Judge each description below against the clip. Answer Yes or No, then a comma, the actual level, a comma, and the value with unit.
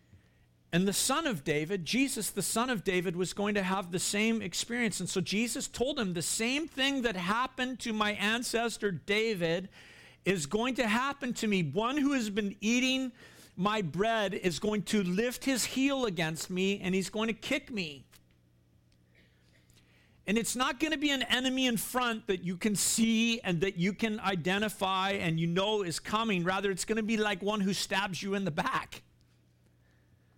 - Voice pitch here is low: No, high, 205 Hz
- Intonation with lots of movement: No, average, 4.2 semitones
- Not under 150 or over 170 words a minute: No, average, 190 wpm